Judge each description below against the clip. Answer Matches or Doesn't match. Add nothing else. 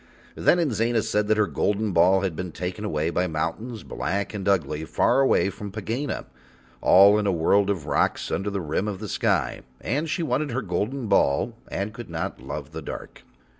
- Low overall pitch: Matches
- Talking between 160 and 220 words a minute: Matches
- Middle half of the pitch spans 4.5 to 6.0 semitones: Doesn't match